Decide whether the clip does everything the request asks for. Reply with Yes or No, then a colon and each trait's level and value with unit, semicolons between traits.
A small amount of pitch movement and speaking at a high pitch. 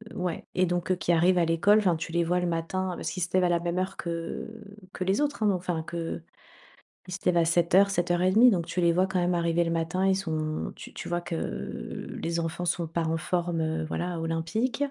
No: narrow, 1.8 semitones; medium, 175 Hz